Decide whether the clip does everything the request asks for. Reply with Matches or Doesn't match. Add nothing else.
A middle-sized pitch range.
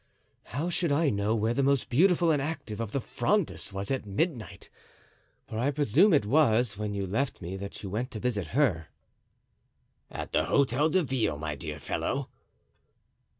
Doesn't match